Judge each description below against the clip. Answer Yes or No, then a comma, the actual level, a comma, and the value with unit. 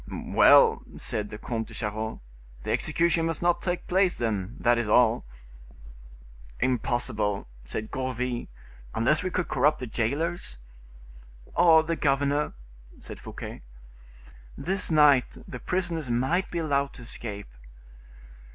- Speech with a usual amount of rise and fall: No, wide, 6.1 semitones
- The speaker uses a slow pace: Yes, slow, 125 wpm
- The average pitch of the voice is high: No, low, 130 Hz